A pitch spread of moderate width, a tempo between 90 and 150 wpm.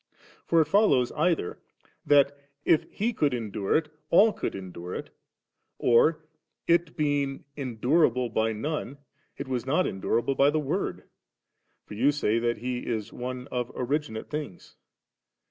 Yes: average, 4.5 semitones; average, 145 wpm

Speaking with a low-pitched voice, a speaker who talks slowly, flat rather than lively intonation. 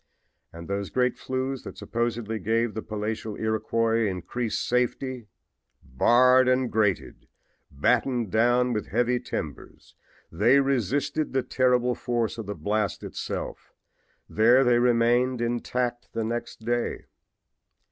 Yes: low, 120 Hz; slow, 120 wpm; narrow, 2.3 semitones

